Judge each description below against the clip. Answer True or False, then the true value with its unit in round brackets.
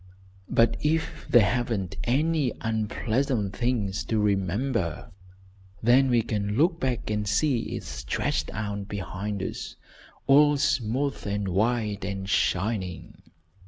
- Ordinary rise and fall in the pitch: True (4.2 semitones)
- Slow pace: True (125 wpm)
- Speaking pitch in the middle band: False (110 Hz)